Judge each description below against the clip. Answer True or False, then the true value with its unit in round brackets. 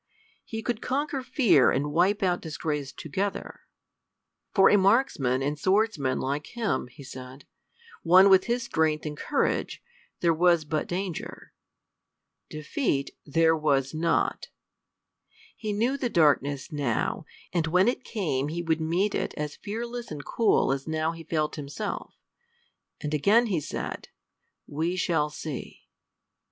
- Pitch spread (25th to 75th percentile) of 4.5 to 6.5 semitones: True (5.4 semitones)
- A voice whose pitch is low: False (165 Hz)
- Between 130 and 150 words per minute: True (140 wpm)